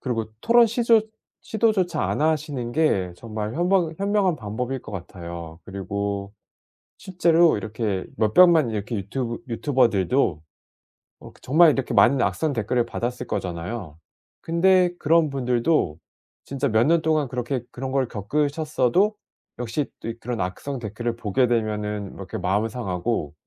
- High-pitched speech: No, low, 125 Hz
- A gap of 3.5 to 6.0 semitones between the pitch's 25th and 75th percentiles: No, wide, 7.0 semitones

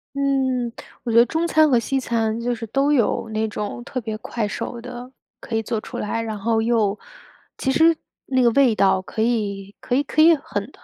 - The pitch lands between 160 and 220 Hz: No, high, 235 Hz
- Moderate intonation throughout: Yes, average, 3.3 semitones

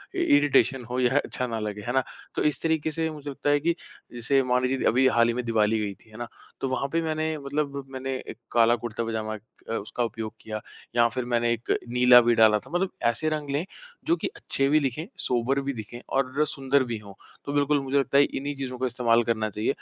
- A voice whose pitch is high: No, low, 130 Hz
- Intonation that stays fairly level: No, average, 3.4 semitones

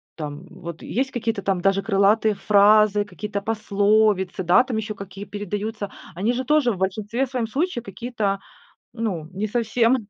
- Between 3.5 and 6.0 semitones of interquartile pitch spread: No, narrow, 2.6 semitones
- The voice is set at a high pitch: Yes, high, 210 Hz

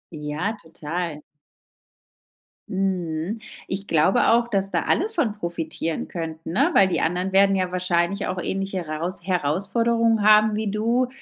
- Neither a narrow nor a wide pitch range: Yes, average, 4.0 semitones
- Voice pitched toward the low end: No, high, 190 Hz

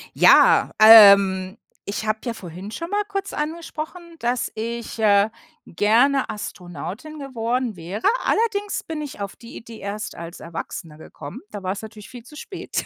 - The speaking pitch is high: Yes, high, 225 Hz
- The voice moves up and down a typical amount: No, wide, 5.8 semitones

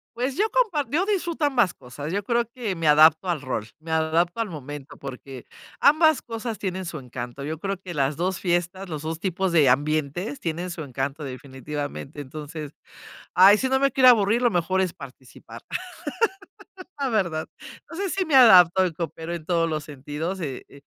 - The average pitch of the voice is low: No, medium, 170 Hz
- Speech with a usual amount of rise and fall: No, wide, 7.0 semitones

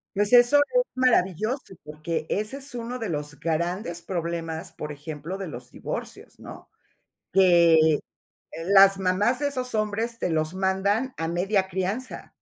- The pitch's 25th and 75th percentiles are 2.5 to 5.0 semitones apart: No, wide, 5.4 semitones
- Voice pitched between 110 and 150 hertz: No, high, 190 Hz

